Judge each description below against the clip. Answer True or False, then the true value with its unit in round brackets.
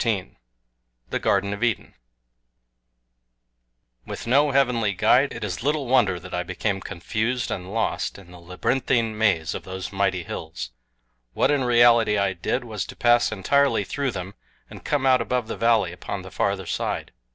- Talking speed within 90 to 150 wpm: False (165 wpm)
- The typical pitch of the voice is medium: False (110 Hz)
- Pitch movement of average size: True (4.5 semitones)